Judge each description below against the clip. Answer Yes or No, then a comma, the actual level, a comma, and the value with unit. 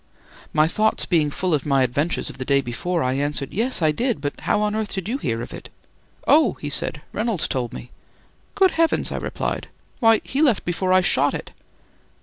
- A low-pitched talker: No, medium, 175 Hz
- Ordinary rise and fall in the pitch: No, wide, 7.5 semitones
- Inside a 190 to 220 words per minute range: Yes, fast, 205 wpm